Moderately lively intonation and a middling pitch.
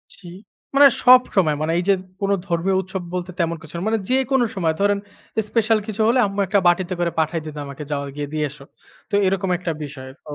Yes: average, 4.2 semitones; medium, 180 Hz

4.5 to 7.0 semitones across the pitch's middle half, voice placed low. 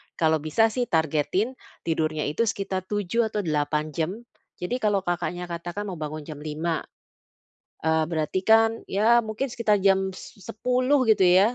No: wide, 5.6 semitones; medium, 185 Hz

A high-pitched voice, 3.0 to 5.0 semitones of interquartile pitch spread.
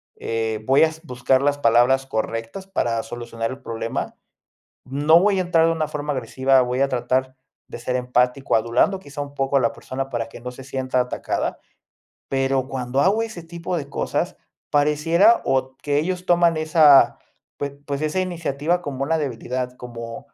No: low, 135 Hz; average, 4.1 semitones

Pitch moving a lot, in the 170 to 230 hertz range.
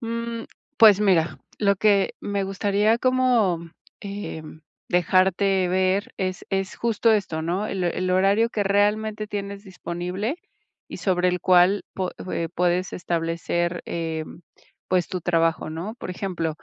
No: average, 2.7 semitones; high, 190 Hz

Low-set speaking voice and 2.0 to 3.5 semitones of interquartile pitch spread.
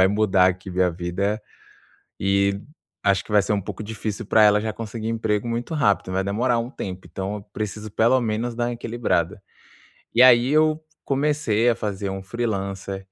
Yes: low, 105 Hz; average, 3.2 semitones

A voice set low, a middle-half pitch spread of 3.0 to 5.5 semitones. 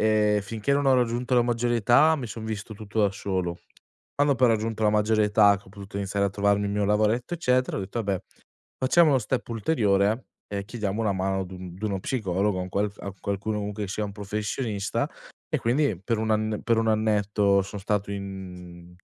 No: low, 105 Hz; narrow, 2.5 semitones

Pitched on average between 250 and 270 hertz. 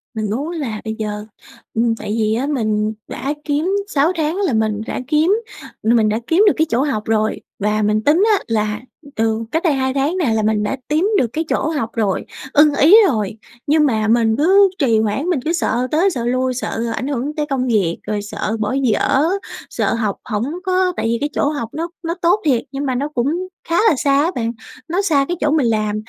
Yes: very high, 255 Hz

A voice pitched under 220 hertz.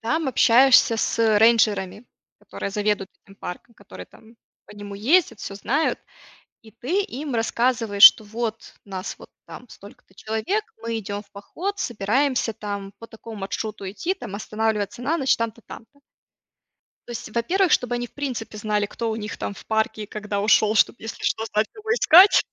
No: high, 225 Hz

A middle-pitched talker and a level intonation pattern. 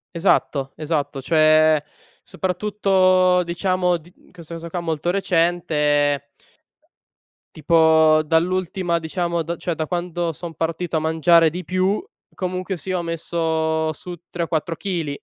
Yes: medium, 170 Hz; narrow, 2.2 semitones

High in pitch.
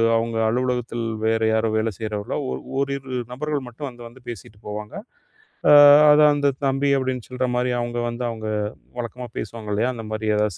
No: low, 120 Hz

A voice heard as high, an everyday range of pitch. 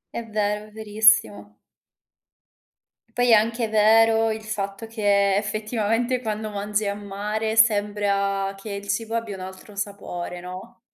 No: high, 210 Hz; narrow, 1.7 semitones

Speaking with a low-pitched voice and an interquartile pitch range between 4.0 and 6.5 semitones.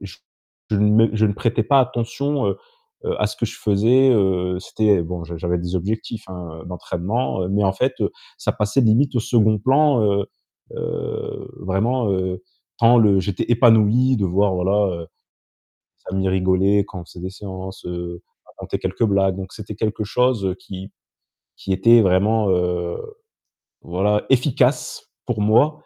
No: low, 100 Hz; average, 3.5 semitones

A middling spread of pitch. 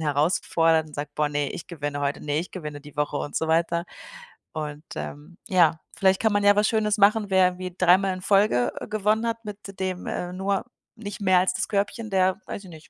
Yes: average, 4.7 semitones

